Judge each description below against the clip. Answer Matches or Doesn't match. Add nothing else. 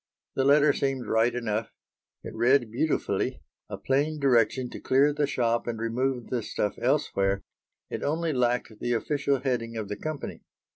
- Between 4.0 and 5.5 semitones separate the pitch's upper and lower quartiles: Doesn't match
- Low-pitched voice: Matches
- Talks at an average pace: Matches